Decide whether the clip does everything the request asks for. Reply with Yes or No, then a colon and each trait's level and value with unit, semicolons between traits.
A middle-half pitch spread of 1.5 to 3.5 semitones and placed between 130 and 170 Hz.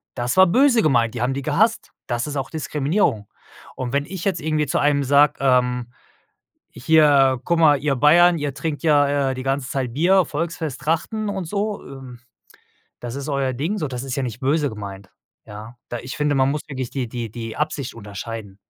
No: average, 3.9 semitones; medium, 140 Hz